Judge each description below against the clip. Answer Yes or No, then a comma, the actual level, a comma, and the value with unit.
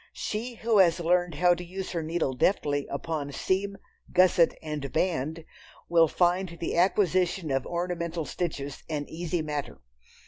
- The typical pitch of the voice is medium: Yes, medium, 170 Hz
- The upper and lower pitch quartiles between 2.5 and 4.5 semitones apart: Yes, average, 2.9 semitones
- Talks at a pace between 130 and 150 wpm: Yes, average, 145 wpm